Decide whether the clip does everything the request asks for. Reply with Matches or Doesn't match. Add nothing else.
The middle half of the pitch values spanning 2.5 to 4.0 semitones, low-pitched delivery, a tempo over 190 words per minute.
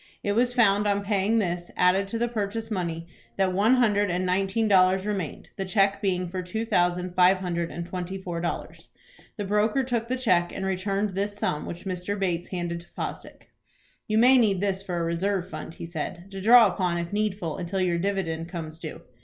Doesn't match